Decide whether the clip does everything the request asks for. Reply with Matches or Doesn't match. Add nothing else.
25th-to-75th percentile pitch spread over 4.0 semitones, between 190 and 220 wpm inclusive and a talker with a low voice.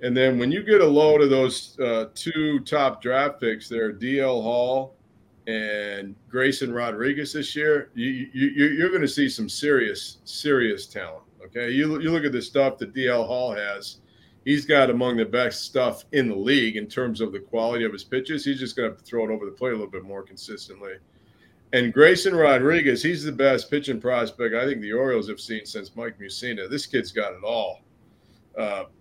Matches